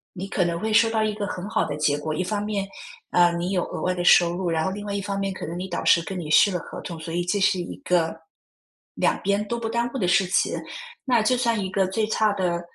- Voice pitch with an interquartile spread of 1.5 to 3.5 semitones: Yes, average, 3.1 semitones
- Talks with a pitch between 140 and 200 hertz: Yes, high, 190 Hz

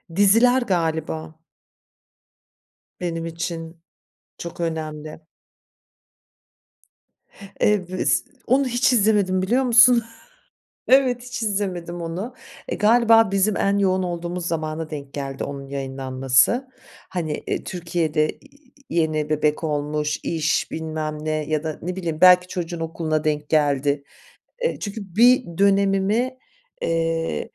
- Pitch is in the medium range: Yes, medium, 170 Hz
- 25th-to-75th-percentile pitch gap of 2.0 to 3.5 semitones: No, average, 4.7 semitones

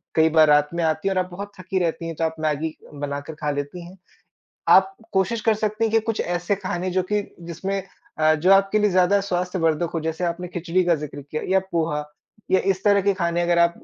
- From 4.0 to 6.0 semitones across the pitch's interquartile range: No, average, 3.2 semitones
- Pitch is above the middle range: No, medium, 175 Hz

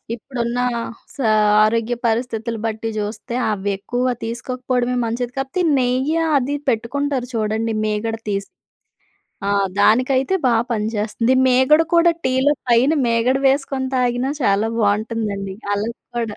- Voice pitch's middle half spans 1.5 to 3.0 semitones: Yes, average, 2.7 semitones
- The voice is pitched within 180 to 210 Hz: No, high, 235 Hz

